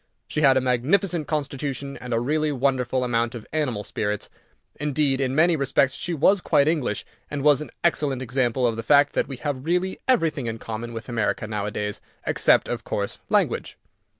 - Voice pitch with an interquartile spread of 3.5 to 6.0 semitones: Yes, average, 4.1 semitones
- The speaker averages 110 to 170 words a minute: No, average, 180 wpm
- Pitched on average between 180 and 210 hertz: No, low, 135 Hz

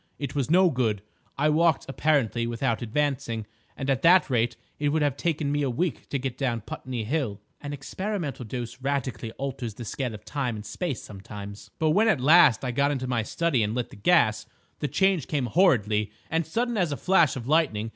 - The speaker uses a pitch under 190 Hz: Yes, low, 135 Hz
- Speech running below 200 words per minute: No, fast, 205 wpm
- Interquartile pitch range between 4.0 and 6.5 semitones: Yes, average, 5.0 semitones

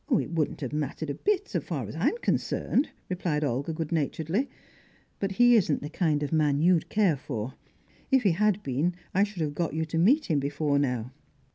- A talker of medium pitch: Yes, medium, 160 Hz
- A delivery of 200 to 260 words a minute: Yes, fast, 205 wpm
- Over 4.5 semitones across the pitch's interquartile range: Yes, average, 5.1 semitones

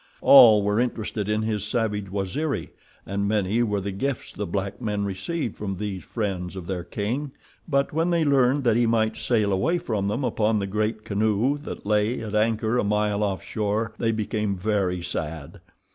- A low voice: Yes, low, 105 Hz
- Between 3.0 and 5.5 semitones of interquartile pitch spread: No, narrow, 2.6 semitones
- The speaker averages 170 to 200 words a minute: Yes, average, 185 wpm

